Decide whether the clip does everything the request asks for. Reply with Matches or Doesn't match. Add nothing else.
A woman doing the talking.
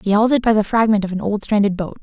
Matches